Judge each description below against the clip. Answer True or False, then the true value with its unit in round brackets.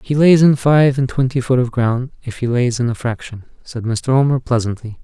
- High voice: False (125 Hz)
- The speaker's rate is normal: False (240 wpm)